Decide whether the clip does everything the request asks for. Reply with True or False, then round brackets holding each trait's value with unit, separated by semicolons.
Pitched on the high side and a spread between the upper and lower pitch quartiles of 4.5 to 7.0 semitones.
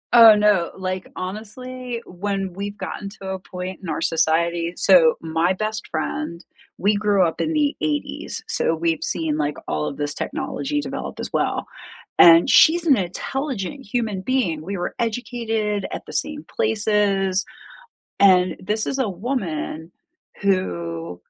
True (195 Hz; 4.8 semitones)